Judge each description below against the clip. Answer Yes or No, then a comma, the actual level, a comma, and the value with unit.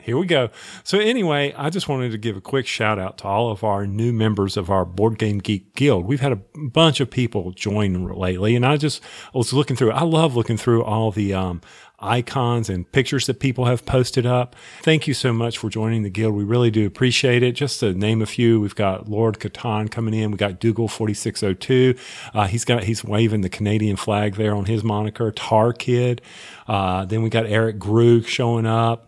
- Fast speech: Yes, fast, 225 wpm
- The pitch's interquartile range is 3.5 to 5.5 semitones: No, average, 3.1 semitones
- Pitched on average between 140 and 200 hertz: No, low, 115 Hz